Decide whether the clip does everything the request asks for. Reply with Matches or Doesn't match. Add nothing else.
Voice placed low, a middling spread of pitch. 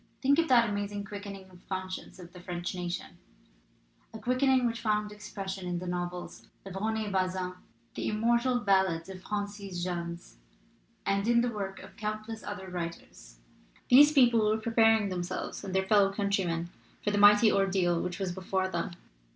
Doesn't match